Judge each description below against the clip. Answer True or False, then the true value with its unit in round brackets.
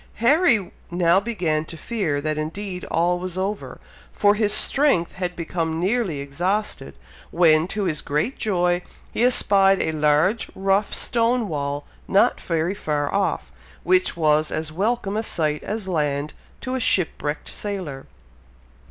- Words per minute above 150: False (145 wpm)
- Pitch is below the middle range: False (180 Hz)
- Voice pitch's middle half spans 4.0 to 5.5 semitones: True (4.8 semitones)